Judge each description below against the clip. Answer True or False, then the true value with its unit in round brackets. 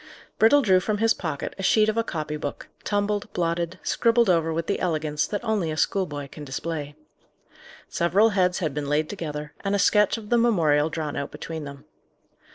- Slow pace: False (190 wpm)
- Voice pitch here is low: False (170 Hz)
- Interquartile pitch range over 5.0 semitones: True (5.4 semitones)